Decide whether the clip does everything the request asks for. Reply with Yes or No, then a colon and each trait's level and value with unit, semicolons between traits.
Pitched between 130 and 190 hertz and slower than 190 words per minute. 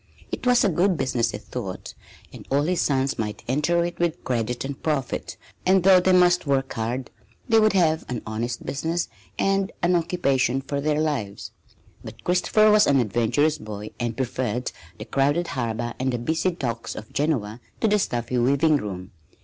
Yes: medium, 140 Hz; average, 180 wpm